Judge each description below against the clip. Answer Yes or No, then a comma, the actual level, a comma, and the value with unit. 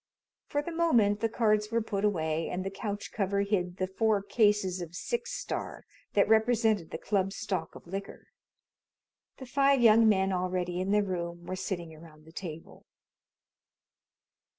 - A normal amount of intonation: Yes, average, 3.5 semitones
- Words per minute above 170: No, average, 160 wpm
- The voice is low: No, high, 200 Hz